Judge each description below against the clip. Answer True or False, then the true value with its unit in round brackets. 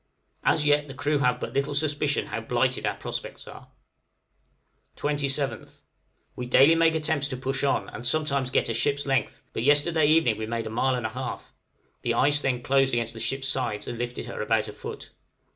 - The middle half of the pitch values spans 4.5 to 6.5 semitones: False (3.3 semitones)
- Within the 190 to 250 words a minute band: True (195 wpm)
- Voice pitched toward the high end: False (135 Hz)